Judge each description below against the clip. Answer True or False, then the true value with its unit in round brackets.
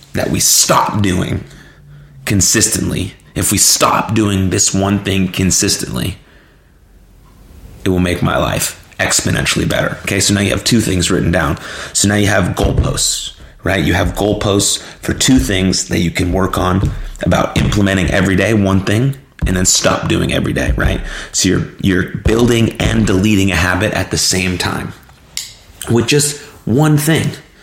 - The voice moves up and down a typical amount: True (3.0 semitones)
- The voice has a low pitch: True (95 Hz)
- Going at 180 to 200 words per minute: False (165 wpm)